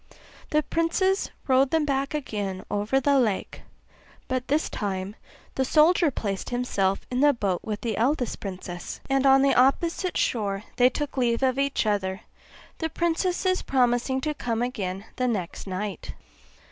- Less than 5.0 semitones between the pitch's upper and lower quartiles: No, wide, 5.6 semitones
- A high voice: Yes, very high, 250 Hz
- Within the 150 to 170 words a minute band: Yes, average, 155 wpm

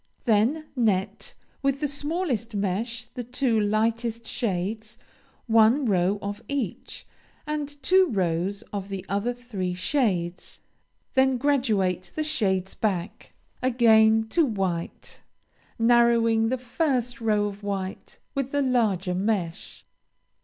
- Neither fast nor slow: No, slow, 115 wpm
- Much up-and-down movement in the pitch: No, average, 4.3 semitones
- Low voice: No, high, 225 Hz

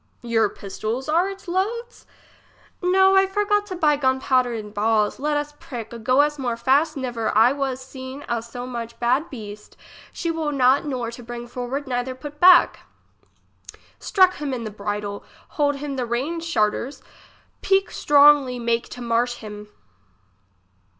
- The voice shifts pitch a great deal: No, average, 4.1 semitones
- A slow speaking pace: No, average, 165 wpm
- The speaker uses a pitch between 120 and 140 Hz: No, very high, 260 Hz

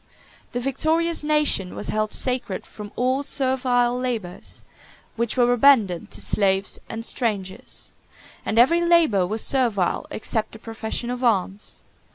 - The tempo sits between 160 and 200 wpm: No, slow, 135 wpm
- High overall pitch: Yes, high, 240 Hz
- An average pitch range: Yes, average, 3.8 semitones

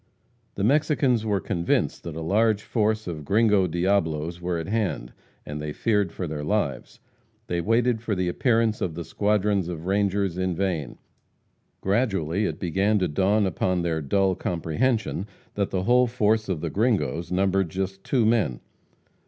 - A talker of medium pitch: No, very low, 95 Hz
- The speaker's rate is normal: Yes, average, 160 wpm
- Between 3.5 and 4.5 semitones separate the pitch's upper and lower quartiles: Yes, average, 3.9 semitones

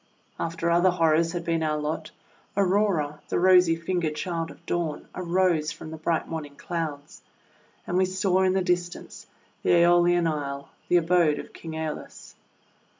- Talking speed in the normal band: Yes, average, 160 wpm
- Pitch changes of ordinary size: No, narrow, 2.2 semitones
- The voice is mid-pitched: Yes, medium, 170 Hz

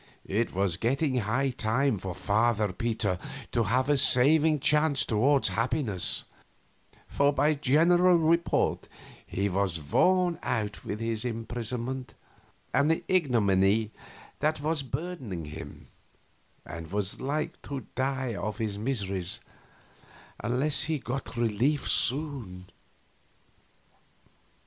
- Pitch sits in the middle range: No, low, 125 Hz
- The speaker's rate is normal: No, slow, 110 wpm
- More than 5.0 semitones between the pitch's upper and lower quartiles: Yes, wide, 5.6 semitones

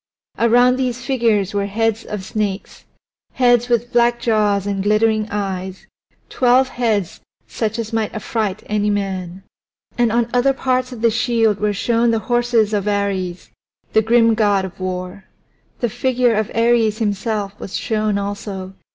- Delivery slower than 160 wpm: Yes, average, 150 wpm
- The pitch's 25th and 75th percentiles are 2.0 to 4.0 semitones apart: Yes, average, 2.8 semitones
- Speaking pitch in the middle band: No, high, 220 Hz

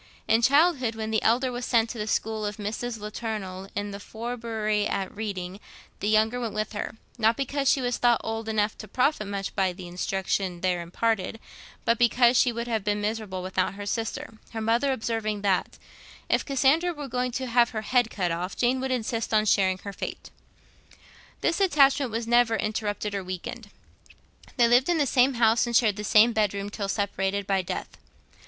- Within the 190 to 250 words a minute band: Yes, average, 195 wpm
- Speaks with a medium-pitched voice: No, high, 220 Hz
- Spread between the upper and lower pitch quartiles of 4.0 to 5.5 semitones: No, average, 3.0 semitones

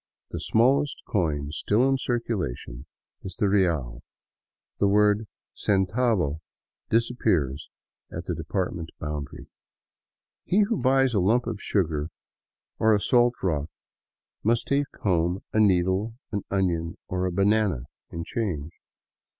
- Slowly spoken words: Yes, slow, 125 wpm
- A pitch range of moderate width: No, wide, 5.7 semitones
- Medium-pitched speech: No, low, 100 Hz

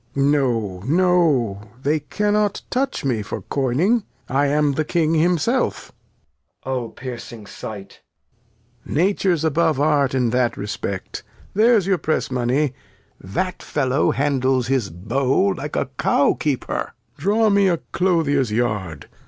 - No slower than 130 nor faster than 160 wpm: Yes, slow, 135 wpm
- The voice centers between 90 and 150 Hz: Yes, medium, 140 Hz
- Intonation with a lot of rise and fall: Yes, wide, 5.8 semitones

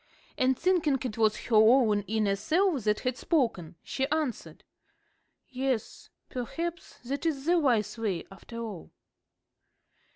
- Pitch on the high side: Yes, very high, 250 Hz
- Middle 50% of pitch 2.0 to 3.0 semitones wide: No, average, 5.3 semitones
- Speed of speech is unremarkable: No, slow, 130 wpm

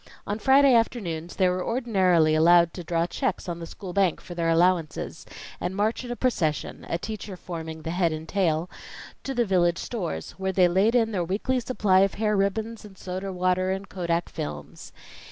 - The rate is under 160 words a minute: No, average, 190 wpm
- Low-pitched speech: No, medium, 185 Hz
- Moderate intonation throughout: Yes, average, 3.7 semitones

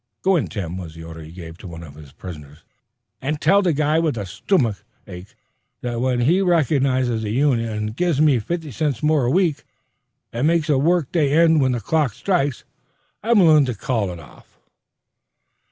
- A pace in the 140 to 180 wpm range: No, average, 195 wpm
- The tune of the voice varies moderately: No, wide, 7.7 semitones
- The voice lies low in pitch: Yes, low, 130 Hz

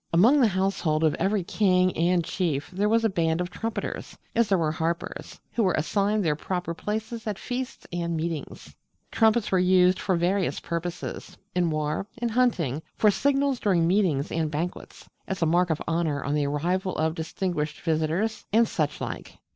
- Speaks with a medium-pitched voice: Yes, medium, 180 Hz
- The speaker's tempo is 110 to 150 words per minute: No, average, 180 wpm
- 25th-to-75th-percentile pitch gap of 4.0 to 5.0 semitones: Yes, average, 4.4 semitones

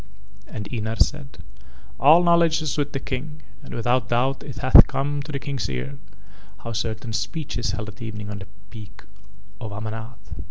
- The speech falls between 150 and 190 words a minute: Yes, average, 175 wpm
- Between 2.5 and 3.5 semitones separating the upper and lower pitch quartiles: No, average, 4.5 semitones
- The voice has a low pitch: Yes, low, 120 Hz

